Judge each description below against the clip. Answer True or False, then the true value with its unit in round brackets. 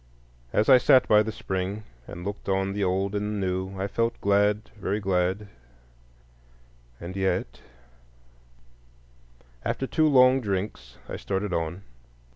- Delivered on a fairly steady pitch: True (2.1 semitones)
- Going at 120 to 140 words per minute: True (135 wpm)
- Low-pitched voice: True (100 Hz)